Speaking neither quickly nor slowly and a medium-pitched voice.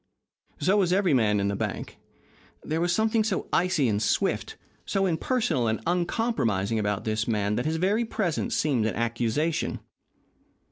Yes: average, 155 wpm; medium, 155 Hz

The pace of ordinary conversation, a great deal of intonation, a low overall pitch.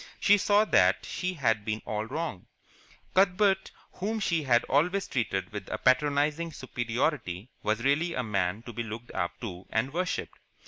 Yes: average, 165 wpm; wide, 7.7 semitones; low, 130 Hz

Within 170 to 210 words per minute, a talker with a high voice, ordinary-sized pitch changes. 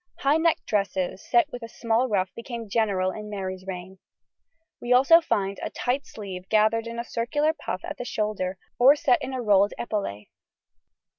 Yes: average, 175 wpm; high, 220 Hz; average, 4.4 semitones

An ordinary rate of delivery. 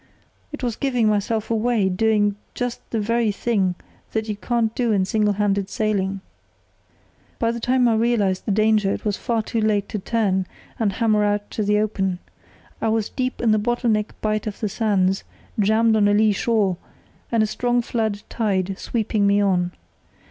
Yes: average, 185 wpm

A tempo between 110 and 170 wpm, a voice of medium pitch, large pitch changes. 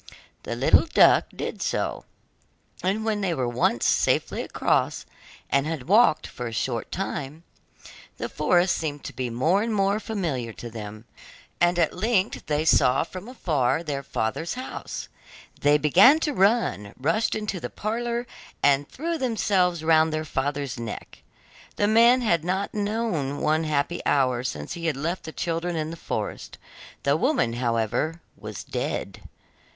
Yes: average, 160 wpm; medium, 160 Hz; wide, 6.8 semitones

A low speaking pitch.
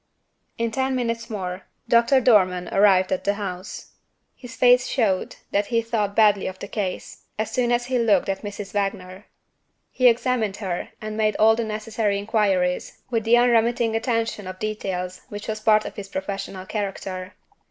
No: high, 215 Hz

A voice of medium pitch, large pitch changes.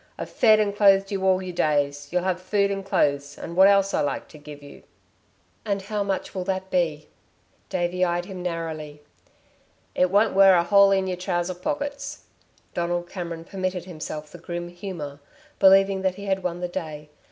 No: medium, 180 Hz; narrow, 2.5 semitones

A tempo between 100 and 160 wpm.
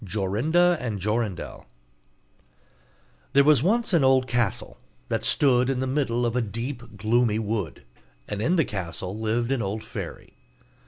Yes: average, 150 wpm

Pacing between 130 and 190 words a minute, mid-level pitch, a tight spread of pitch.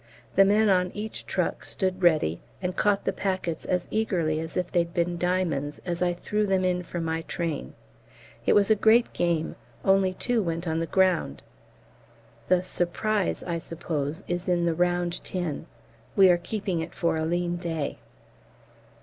Yes: average, 170 wpm; medium, 175 Hz; narrow, 2.2 semitones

